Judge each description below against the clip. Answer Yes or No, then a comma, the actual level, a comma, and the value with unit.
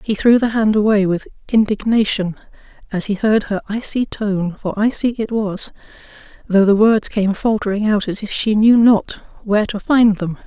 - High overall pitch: Yes, high, 210 Hz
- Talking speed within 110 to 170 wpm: No, average, 185 wpm